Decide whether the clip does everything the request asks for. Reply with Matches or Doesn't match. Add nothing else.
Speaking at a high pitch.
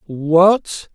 Doesn't match